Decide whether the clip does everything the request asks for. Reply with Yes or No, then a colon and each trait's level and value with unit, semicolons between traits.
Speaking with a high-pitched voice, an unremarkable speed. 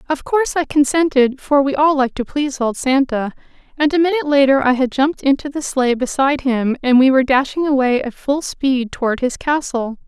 No: very high, 270 Hz; fast, 210 wpm